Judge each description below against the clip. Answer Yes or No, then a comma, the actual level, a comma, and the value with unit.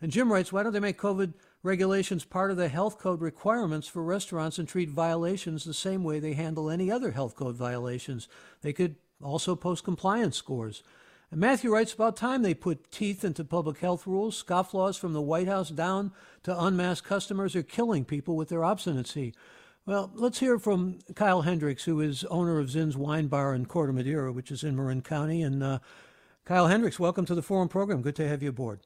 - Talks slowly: No, fast, 205 wpm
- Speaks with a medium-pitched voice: Yes, medium, 175 Hz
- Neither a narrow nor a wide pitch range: Yes, average, 4.2 semitones